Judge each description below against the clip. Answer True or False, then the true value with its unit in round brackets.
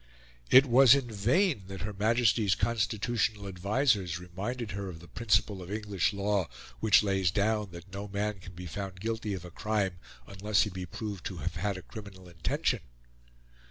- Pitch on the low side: True (100 Hz)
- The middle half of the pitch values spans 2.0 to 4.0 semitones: True (2.7 semitones)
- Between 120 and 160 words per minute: False (175 wpm)